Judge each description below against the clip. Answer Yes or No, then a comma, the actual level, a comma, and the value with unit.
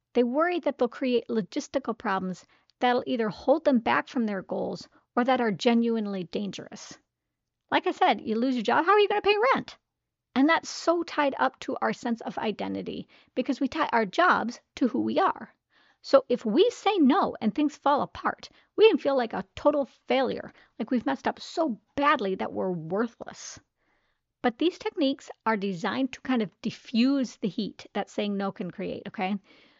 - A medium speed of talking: Yes, average, 190 wpm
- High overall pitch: Yes, very high, 250 Hz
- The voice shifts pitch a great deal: No, average, 4.8 semitones